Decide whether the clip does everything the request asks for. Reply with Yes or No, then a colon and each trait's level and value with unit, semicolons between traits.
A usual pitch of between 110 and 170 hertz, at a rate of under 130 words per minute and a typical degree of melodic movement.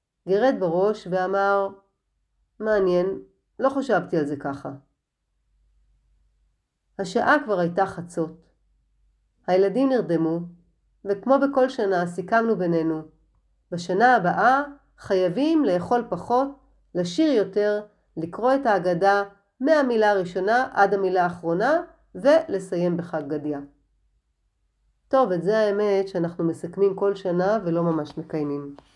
No: high, 190 Hz; slow, 100 wpm; average, 4.4 semitones